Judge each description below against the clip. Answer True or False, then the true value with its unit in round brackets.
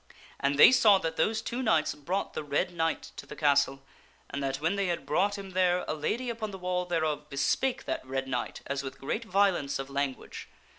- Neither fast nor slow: False (210 wpm)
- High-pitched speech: False (165 Hz)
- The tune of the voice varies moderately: False (5.9 semitones)